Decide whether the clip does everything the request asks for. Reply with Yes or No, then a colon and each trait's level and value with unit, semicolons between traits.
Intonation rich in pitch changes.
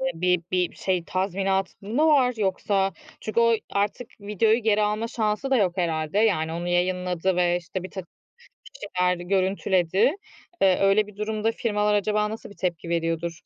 No: average, 2.9 semitones